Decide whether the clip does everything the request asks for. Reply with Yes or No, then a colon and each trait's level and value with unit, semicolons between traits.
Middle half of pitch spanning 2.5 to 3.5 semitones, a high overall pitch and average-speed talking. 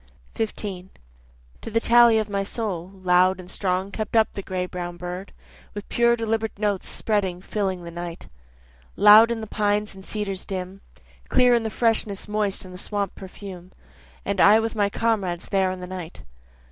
Yes: average, 3.0 semitones; high, 200 Hz; average, 175 wpm